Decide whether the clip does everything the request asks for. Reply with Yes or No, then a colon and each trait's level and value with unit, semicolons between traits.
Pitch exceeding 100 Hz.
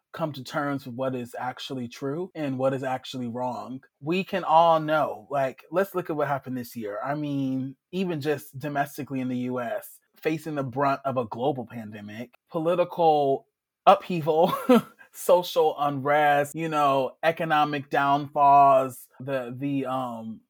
Yes: medium, 140 Hz